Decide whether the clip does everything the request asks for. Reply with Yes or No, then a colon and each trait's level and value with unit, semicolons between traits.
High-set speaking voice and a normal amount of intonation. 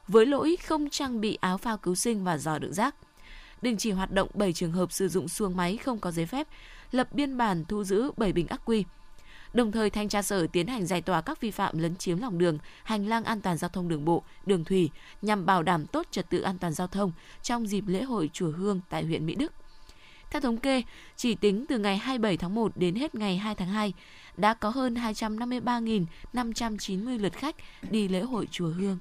Yes: high, 200 Hz; average, 4.4 semitones